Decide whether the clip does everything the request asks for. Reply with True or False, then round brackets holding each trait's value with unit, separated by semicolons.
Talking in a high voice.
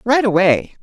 True (220 Hz)